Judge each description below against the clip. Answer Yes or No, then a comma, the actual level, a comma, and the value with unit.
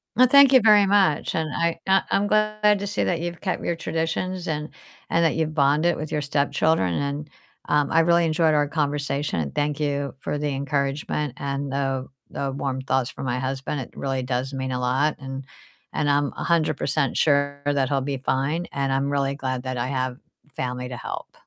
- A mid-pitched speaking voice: Yes, medium, 145 Hz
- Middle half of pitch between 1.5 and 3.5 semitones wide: Yes, average, 3.2 semitones